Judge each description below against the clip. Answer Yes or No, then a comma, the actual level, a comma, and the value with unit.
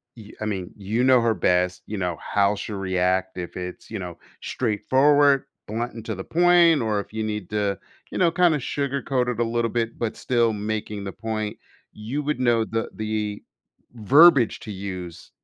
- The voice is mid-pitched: No, low, 110 Hz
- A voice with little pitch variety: No, average, 3.9 semitones